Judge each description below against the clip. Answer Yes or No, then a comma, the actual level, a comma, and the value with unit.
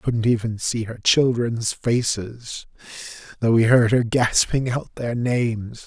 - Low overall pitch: Yes, low, 115 Hz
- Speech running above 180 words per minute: No, average, 155 wpm